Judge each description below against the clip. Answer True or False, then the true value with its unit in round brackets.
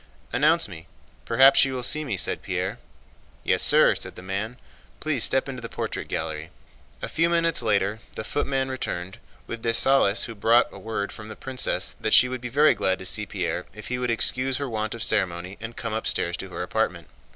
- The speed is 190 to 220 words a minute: True (200 wpm)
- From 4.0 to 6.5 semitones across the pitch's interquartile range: True (4.5 semitones)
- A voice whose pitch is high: False (115 Hz)